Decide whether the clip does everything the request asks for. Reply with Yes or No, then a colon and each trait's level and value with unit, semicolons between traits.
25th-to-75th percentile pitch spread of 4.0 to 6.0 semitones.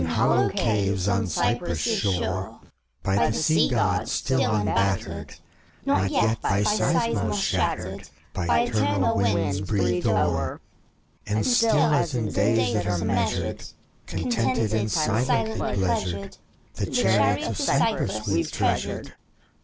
No: average, 3.0 semitones